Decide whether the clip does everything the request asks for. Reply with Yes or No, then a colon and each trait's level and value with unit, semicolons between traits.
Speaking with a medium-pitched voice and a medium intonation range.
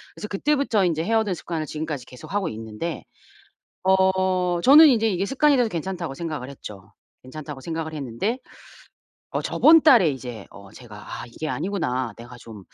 No: medium, 165 Hz; wide, 7.7 semitones